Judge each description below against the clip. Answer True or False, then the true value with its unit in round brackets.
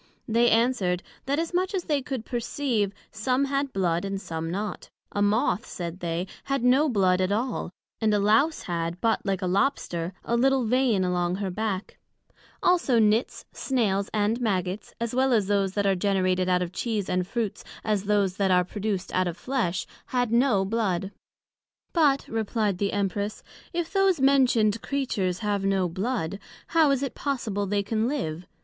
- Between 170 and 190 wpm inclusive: True (175 wpm)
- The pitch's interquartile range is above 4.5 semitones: True (5.1 semitones)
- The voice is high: True (210 Hz)